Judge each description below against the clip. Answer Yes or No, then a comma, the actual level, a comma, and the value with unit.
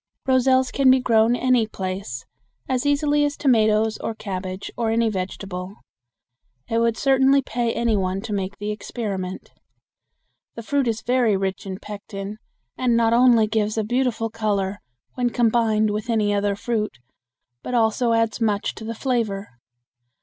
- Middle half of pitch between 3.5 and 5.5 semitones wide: No, average, 3.0 semitones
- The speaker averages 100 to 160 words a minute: Yes, average, 155 wpm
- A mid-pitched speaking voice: No, high, 225 Hz